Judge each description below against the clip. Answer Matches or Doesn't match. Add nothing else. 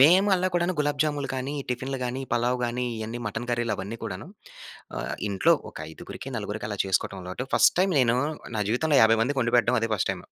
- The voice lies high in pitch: Doesn't match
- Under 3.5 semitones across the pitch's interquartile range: Doesn't match